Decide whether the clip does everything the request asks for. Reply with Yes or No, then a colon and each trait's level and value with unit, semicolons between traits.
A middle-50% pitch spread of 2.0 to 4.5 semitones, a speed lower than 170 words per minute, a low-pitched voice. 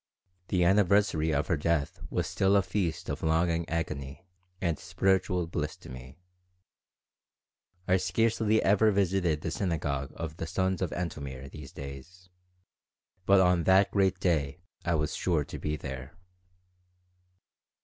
Yes: average, 3.9 semitones; average, 140 wpm; very low, 85 Hz